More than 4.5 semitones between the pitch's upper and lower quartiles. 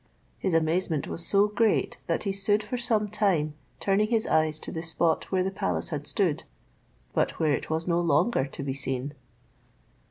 Yes: average, 5.0 semitones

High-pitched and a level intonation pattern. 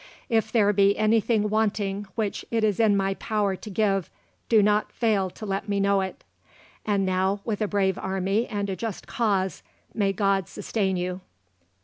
Yes: high, 200 Hz; narrow, 1.9 semitones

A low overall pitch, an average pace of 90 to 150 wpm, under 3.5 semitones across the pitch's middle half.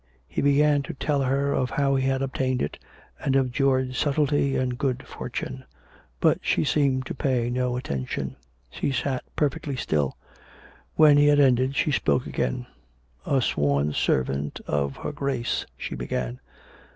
No: low, 130 Hz; average, 165 wpm; average, 2.9 semitones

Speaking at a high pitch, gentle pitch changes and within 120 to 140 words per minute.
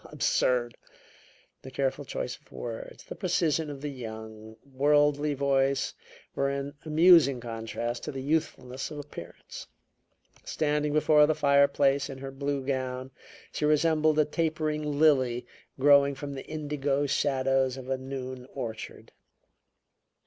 No: medium, 140 Hz; narrow, 2.2 semitones; slow, 135 wpm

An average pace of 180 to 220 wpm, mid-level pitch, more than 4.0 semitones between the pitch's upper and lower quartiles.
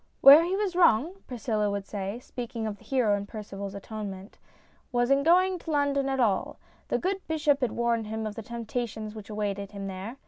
No: average, 200 wpm; high, 230 Hz; average, 5.2 semitones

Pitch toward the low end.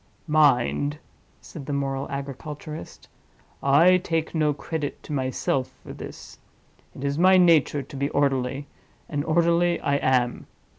No: medium, 145 Hz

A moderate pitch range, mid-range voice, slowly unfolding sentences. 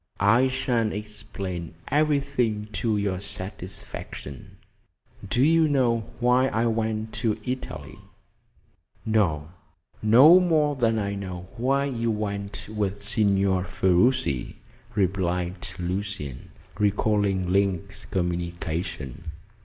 No: average, 4.3 semitones; low, 105 Hz; slow, 100 wpm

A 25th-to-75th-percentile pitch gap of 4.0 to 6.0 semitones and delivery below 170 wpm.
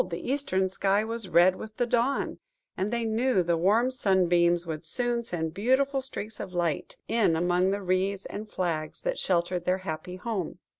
No: average, 4.8 semitones; average, 180 wpm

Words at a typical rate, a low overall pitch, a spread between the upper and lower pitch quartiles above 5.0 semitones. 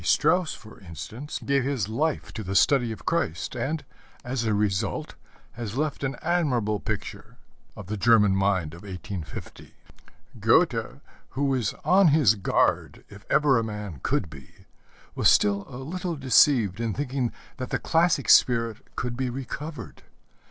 Yes: average, 150 wpm; low, 120 Hz; wide, 5.4 semitones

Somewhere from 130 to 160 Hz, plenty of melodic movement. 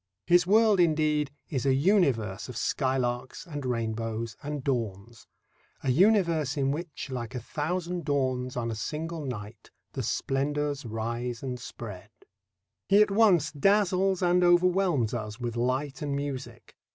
Yes: medium, 140 Hz; wide, 6.0 semitones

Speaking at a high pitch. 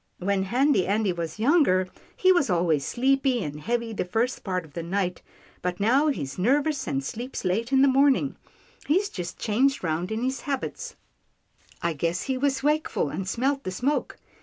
Yes: high, 225 Hz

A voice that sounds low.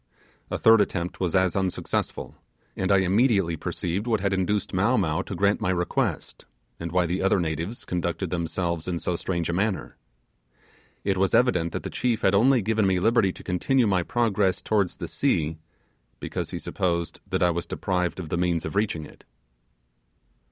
Yes: very low, 95 Hz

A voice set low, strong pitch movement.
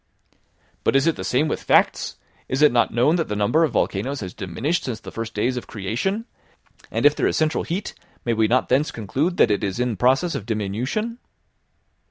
Yes: low, 125 Hz; wide, 6.0 semitones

